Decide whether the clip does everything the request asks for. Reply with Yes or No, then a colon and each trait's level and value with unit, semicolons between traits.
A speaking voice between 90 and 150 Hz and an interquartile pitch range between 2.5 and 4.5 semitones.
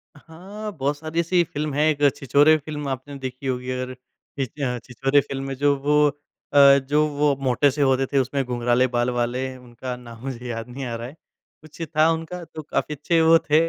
Yes: medium, 140 Hz; average, 3.0 semitones